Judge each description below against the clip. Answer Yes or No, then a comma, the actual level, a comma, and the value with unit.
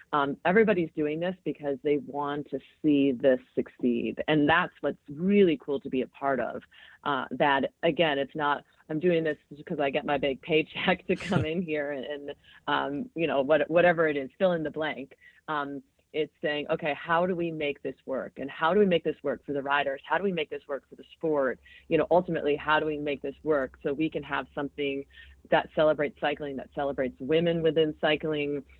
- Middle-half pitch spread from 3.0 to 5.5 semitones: No, narrow, 2.5 semitones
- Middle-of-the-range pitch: Yes, medium, 150 Hz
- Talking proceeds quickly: Yes, fast, 215 wpm